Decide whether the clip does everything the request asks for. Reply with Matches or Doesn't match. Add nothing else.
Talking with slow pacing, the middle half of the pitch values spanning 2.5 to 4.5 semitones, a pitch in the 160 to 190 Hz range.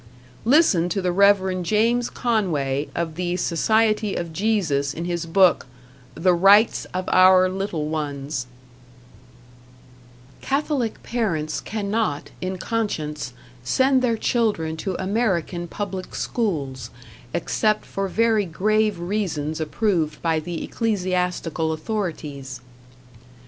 Doesn't match